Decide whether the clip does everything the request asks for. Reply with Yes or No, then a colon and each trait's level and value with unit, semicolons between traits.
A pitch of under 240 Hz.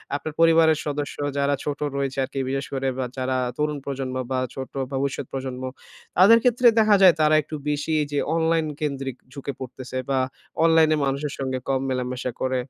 Yes: medium, 140 Hz